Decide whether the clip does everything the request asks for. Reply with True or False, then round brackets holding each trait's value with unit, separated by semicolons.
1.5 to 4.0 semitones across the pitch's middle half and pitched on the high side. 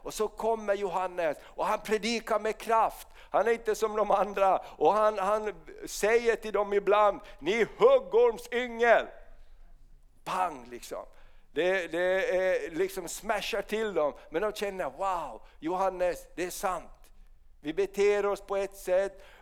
True (2.9 semitones; 210 Hz)